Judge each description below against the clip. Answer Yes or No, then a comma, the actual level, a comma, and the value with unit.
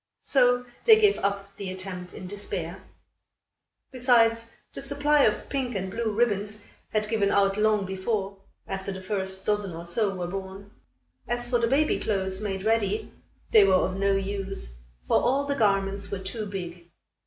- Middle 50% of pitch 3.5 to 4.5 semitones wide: No, average, 3.1 semitones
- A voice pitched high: Yes, high, 200 Hz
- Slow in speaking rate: No, average, 165 wpm